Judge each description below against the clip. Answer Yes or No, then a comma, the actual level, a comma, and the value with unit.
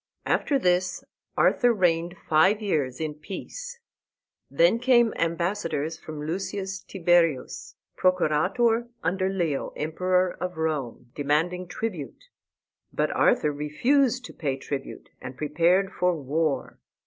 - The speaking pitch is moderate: Yes, medium, 175 Hz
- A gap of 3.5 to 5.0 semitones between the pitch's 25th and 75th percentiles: Yes, average, 4.2 semitones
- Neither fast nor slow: No, slow, 110 wpm